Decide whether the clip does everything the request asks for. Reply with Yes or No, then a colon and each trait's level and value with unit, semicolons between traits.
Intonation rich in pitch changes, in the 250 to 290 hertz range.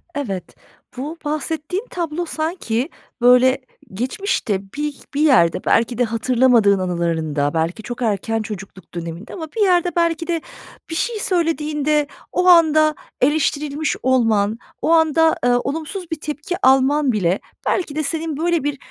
Yes: wide, 6.3 semitones; very high, 285 Hz